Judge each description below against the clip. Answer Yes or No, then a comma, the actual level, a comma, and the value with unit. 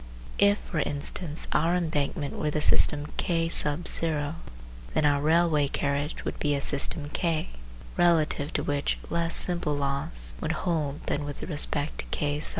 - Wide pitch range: No, narrow, 2.5 semitones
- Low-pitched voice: No, medium, 150 Hz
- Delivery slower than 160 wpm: Yes, average, 150 wpm